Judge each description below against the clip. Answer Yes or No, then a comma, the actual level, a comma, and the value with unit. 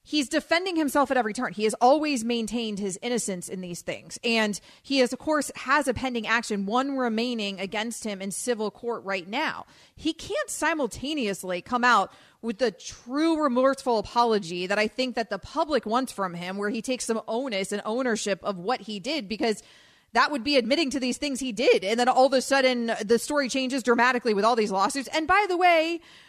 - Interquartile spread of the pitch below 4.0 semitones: No, average, 4.3 semitones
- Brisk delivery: Yes, fast, 210 wpm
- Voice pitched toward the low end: No, high, 245 Hz